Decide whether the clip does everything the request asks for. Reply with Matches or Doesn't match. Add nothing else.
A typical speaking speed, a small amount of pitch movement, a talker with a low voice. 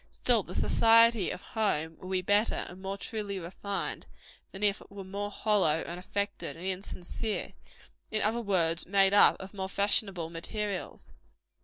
Doesn't match